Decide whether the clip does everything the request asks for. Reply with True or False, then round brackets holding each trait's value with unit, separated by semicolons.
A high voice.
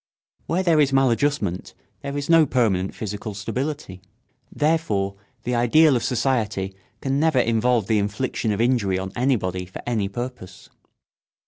False (120 Hz)